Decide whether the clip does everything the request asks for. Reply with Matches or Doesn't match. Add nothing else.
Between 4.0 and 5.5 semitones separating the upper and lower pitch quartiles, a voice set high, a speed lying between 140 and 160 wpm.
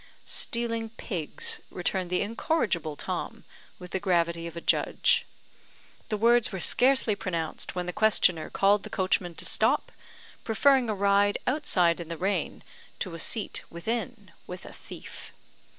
Matches